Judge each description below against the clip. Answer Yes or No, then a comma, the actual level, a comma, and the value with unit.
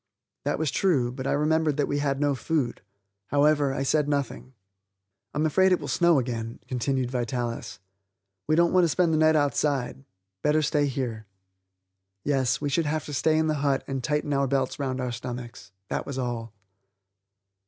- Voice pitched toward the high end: No, medium, 140 Hz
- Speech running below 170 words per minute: No, average, 180 wpm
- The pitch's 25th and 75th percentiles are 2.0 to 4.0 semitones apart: Yes, average, 3.2 semitones